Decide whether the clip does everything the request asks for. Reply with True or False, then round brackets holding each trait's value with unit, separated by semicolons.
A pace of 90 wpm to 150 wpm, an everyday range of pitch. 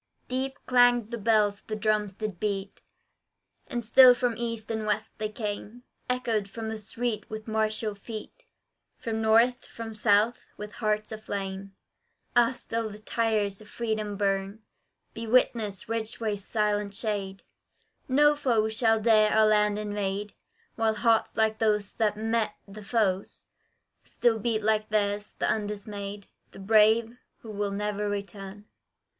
False (140 wpm; 1.7 semitones)